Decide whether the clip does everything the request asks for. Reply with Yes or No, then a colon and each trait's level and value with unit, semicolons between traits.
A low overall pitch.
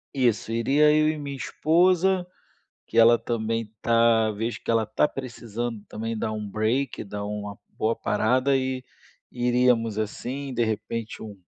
Yes: low, 115 Hz